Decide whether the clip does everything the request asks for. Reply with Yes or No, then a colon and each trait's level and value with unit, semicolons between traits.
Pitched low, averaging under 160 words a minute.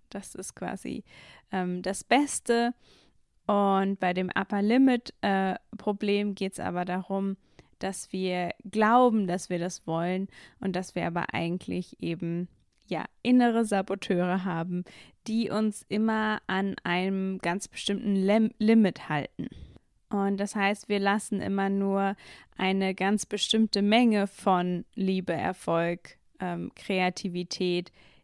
No: high, 195 Hz; average, 130 wpm